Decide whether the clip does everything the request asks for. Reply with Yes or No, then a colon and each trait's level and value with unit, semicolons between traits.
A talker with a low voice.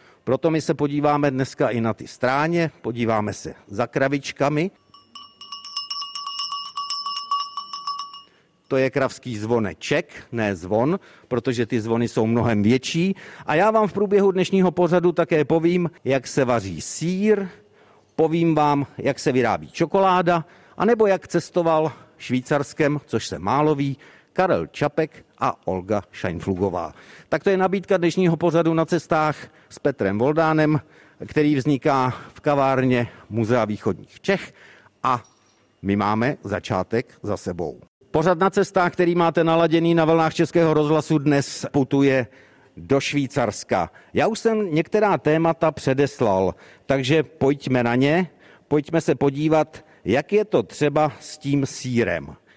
No: medium, 150 Hz